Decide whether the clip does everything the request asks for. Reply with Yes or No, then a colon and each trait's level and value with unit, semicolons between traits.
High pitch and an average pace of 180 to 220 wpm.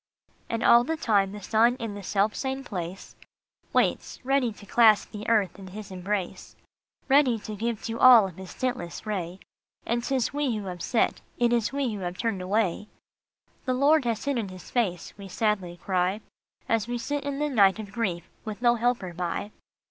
Yes: high, 215 Hz; average, 200 wpm